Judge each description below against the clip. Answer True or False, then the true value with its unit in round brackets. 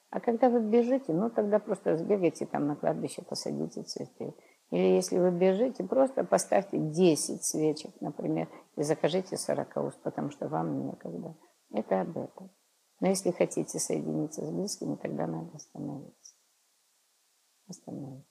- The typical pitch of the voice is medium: True (160 Hz)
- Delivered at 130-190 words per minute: True (140 wpm)